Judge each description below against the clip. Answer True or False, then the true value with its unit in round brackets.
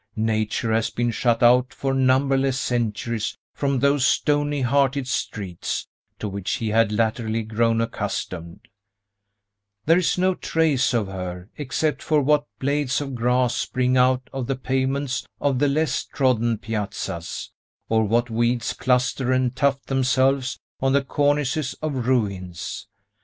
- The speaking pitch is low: True (125 Hz)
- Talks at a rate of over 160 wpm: False (140 wpm)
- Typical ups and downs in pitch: True (3.3 semitones)